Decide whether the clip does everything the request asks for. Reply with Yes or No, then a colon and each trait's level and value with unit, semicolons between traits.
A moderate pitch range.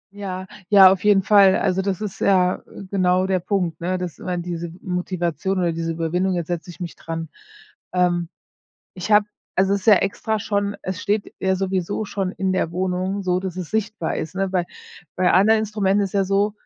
No: narrow, 1.8 semitones